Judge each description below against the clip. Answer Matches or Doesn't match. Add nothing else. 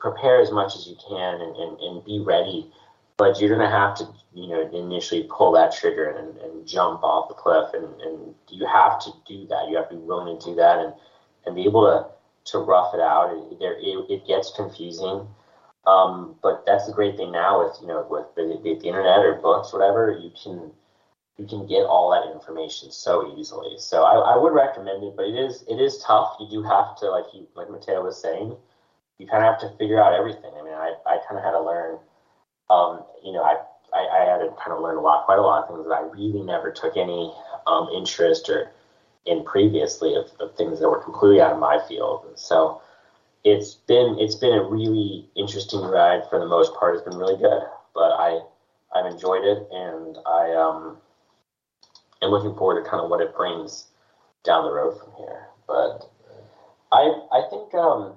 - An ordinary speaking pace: Doesn't match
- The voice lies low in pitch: Matches